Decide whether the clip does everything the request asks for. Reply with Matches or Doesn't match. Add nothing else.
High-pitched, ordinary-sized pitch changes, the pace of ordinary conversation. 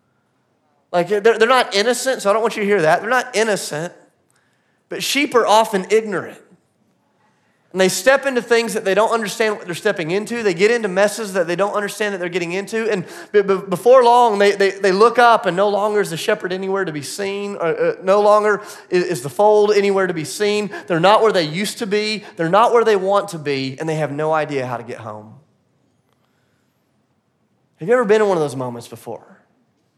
Doesn't match